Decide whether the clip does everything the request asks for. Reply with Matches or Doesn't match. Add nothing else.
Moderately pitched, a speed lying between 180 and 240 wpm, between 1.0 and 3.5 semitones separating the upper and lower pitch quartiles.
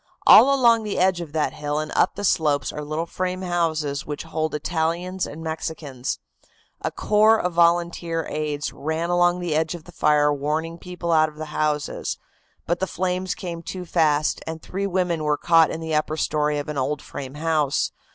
Matches